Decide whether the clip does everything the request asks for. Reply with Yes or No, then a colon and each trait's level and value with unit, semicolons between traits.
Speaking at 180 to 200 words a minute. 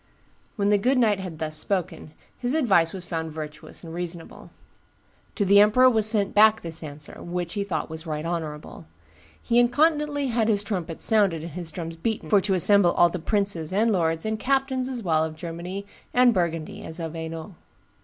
Yes: average, 185 wpm